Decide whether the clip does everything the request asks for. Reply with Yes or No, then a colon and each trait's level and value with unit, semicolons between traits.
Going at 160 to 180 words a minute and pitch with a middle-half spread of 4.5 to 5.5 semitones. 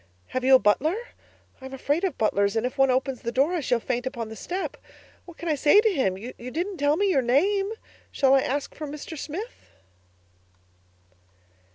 No: average, 195 wpm; average, 4.9 semitones